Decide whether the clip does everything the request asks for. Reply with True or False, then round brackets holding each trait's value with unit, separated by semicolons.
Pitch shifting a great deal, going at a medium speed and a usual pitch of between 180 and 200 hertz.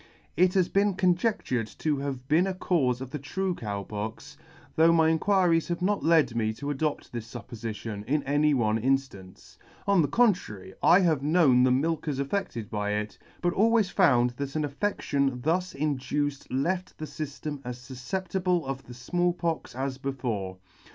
False (5.8 semitones; 170 wpm; 145 Hz)